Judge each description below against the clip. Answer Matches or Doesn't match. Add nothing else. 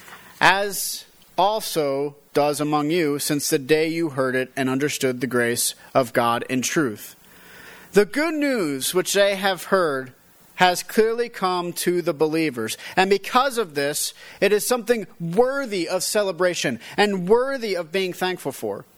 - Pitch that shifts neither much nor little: Doesn't match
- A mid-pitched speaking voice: Matches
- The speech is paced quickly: Doesn't match